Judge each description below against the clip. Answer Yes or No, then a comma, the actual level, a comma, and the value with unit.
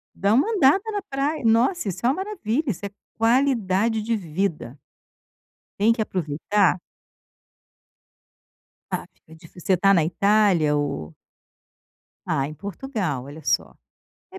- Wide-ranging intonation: Yes, wide, 7.2 semitones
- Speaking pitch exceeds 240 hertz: No, high, 205 Hz